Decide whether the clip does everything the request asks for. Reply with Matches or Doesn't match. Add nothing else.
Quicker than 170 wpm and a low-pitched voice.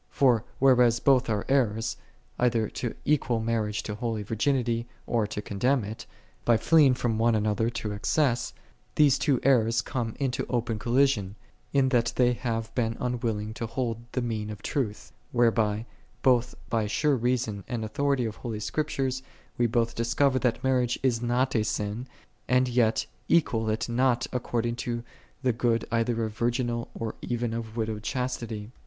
Doesn't match